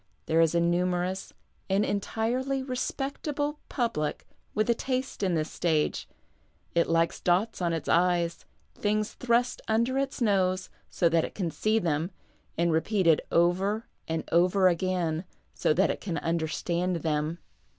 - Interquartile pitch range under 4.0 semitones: No, average, 4.7 semitones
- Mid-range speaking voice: Yes, medium, 180 Hz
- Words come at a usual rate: Yes, average, 150 wpm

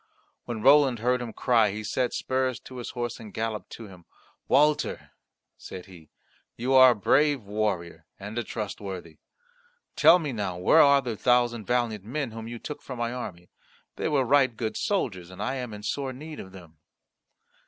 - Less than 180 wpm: No, average, 185 wpm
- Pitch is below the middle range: Yes, low, 120 Hz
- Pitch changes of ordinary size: Yes, average, 4.0 semitones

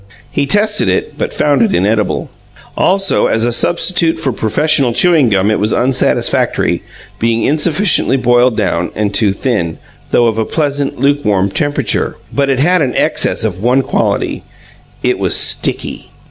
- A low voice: Yes, low, 130 Hz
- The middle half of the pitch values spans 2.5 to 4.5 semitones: No, wide, 5.6 semitones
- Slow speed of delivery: No, average, 155 wpm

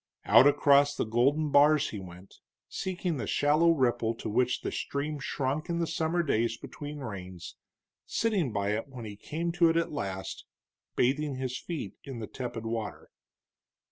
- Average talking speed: Yes, average, 175 wpm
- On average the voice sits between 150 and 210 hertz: No, low, 135 Hz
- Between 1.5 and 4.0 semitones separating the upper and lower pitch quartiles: No, average, 5.3 semitones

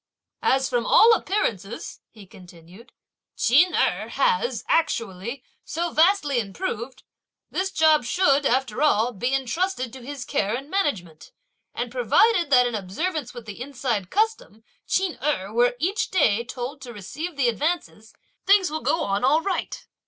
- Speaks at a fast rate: No, average, 150 wpm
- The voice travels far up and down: Yes, wide, 6.9 semitones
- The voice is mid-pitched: No, very high, 265 Hz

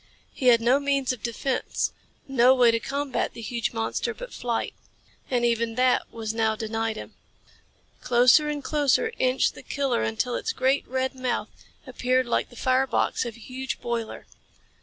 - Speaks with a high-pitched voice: Yes, very high, 250 Hz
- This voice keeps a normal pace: Yes, average, 170 wpm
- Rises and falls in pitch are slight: Yes, narrow, 2.3 semitones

